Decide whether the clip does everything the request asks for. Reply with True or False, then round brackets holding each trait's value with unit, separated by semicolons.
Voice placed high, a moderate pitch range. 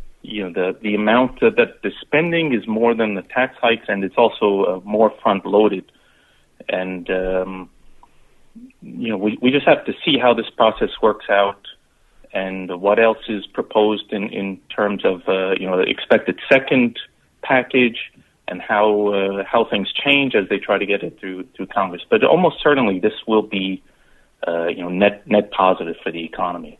False (105 Hz; 3.7 semitones)